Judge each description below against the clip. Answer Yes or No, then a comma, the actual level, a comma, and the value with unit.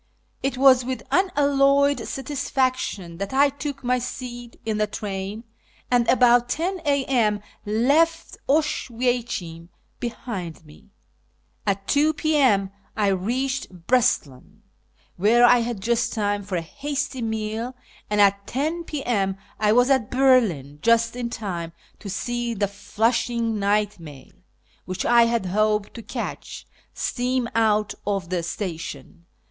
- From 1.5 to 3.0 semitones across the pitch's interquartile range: No, average, 4.5 semitones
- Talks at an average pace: No, slow, 130 wpm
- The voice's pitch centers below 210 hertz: No, high, 230 Hz